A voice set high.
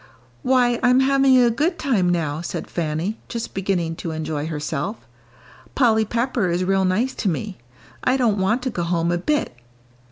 Yes: high, 200 Hz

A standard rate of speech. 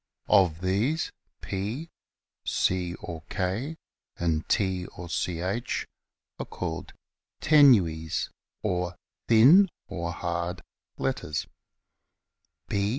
No: slow, 85 wpm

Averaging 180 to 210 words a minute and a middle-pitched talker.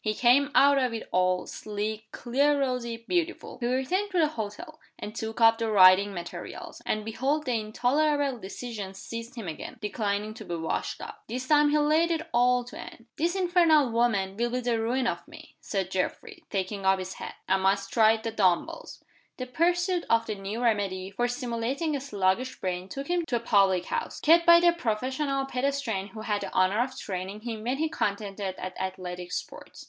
No: average, 195 wpm; high, 230 Hz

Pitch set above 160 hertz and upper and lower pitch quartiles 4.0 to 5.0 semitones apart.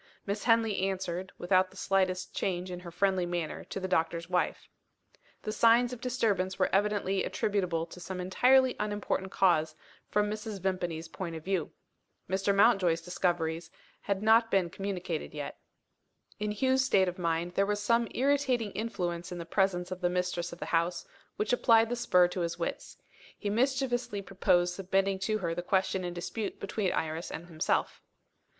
No: high, 190 Hz; average, 3.1 semitones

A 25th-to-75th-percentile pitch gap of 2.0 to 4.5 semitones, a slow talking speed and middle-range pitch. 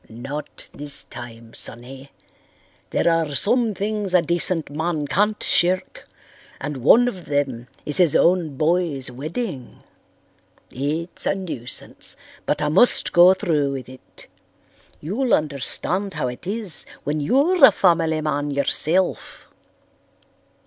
No: average, 4.9 semitones; slow, 125 wpm; medium, 160 Hz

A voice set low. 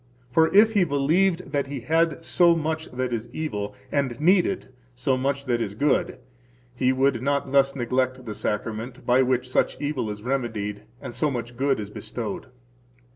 Yes: low, 130 Hz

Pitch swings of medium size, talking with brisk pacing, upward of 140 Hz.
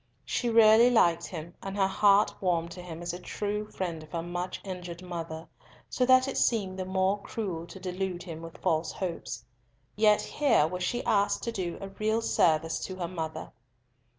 No: average, 3.4 semitones; average, 190 wpm; medium, 185 Hz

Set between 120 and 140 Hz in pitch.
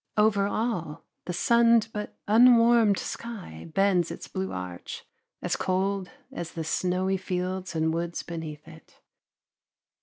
No: medium, 185 Hz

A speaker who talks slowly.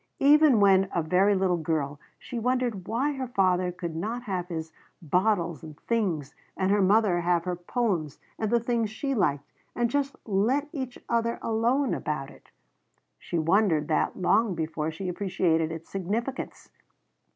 No: average, 160 wpm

